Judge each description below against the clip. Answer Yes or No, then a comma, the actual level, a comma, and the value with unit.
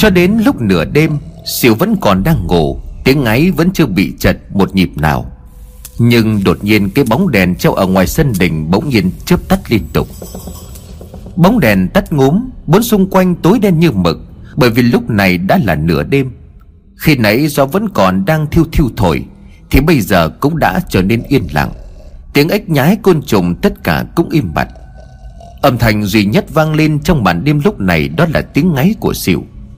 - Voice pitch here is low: Yes, low, 130 Hz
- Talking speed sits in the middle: Yes, average, 200 wpm